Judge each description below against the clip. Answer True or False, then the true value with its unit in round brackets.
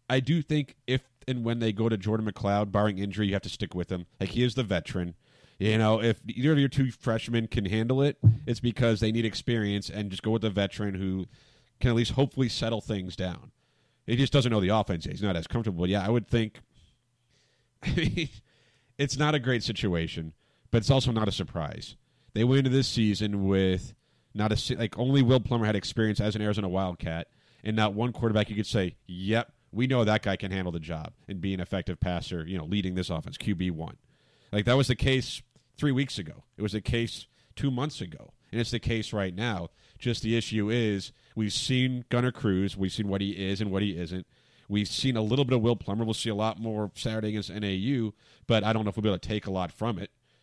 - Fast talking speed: True (230 wpm)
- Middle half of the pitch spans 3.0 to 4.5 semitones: True (3.6 semitones)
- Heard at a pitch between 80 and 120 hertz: True (110 Hz)